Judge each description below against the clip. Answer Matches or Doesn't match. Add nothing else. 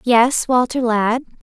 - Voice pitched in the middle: Doesn't match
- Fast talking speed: Doesn't match